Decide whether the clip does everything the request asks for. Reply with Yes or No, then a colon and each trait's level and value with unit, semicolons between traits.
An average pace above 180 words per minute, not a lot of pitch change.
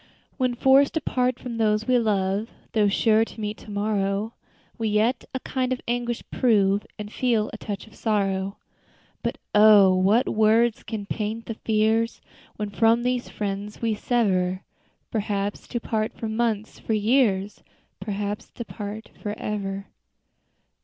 No: average, 155 wpm; narrow, 2.2 semitones